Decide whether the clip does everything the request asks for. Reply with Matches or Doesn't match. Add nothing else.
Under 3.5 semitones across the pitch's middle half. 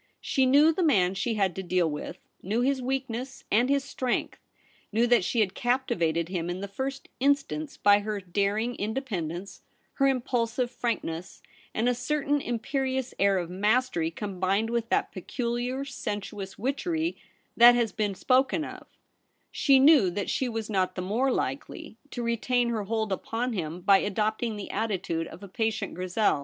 Doesn't match